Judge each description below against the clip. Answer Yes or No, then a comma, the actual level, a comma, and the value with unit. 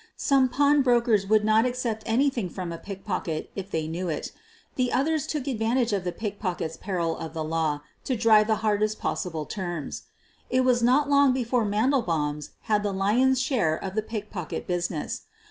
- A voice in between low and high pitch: No, high, 215 Hz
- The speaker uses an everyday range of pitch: No, wide, 6.0 semitones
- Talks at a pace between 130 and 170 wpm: No, average, 180 wpm